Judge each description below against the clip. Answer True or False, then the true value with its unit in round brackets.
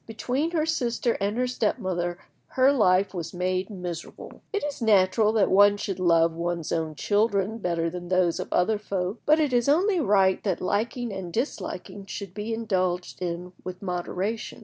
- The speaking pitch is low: False (195 Hz)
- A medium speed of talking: True (175 wpm)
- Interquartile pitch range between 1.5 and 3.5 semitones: False (4.2 semitones)